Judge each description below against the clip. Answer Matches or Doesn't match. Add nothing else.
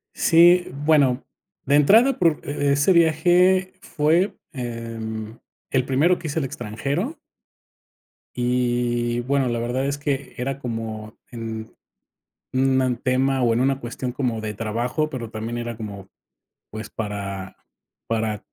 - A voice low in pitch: Matches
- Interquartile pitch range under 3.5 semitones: Doesn't match